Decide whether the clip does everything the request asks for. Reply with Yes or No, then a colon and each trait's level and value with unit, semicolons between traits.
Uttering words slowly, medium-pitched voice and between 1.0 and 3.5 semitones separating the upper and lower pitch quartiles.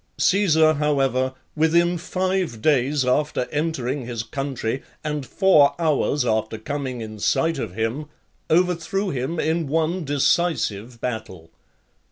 No: slow, 120 wpm; medium, 145 Hz; average, 4.7 semitones